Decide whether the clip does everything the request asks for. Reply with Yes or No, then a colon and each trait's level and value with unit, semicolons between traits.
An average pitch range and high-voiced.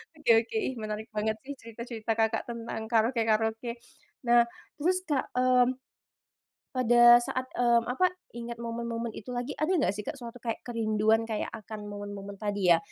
No: narrow, 2.0 semitones; high, 230 Hz